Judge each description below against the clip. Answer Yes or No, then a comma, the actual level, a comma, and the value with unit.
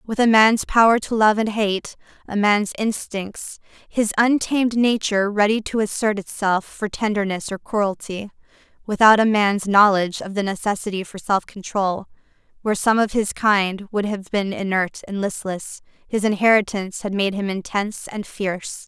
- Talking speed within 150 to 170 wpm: Yes, average, 160 wpm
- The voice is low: No, high, 205 Hz